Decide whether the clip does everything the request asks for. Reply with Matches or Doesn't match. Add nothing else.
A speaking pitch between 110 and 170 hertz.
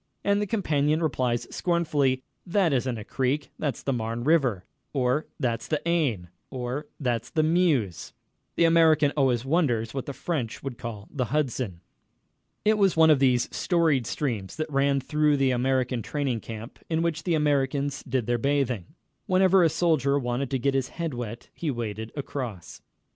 Matches